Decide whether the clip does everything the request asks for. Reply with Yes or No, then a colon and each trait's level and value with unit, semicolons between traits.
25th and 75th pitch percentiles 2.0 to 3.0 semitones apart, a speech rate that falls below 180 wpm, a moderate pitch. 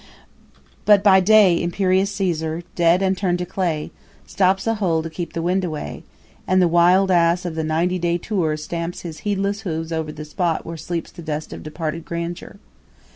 No: narrow, 2.5 semitones; average, 185 wpm; medium, 175 Hz